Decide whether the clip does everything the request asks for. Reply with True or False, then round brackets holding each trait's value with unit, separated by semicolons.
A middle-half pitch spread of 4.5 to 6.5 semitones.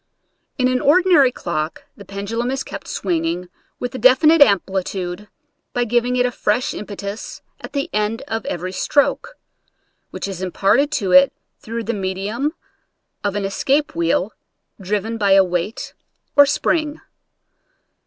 True (5.0 semitones)